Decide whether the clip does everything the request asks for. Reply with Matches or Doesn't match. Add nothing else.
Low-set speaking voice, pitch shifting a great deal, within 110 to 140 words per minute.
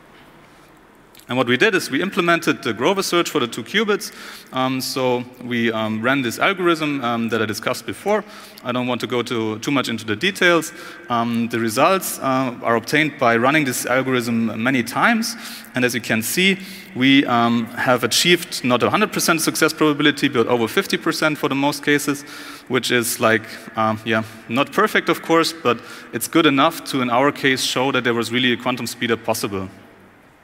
Doesn't match